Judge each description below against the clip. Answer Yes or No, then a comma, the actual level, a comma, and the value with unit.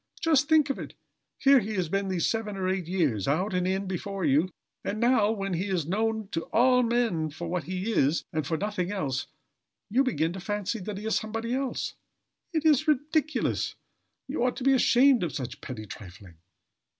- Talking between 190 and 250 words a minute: Yes, average, 200 wpm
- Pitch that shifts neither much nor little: No, wide, 6.0 semitones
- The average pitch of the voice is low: No, high, 200 Hz